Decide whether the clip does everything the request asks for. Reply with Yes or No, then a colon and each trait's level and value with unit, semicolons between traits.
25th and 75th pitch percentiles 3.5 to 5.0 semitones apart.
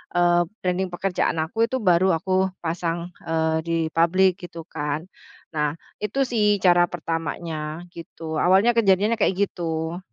No: average, 2.7 semitones